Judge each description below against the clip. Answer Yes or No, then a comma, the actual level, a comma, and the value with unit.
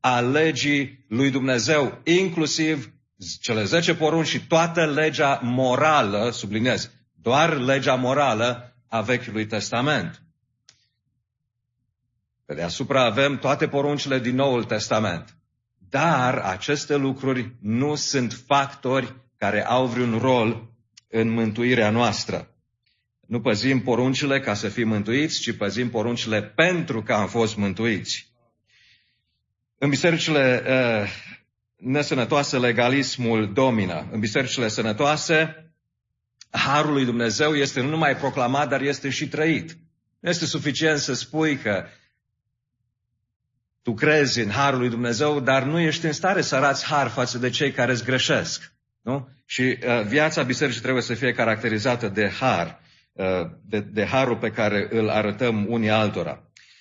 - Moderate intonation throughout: Yes, average, 3.7 semitones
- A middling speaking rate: No, slow, 130 wpm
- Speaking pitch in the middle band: No, low, 125 Hz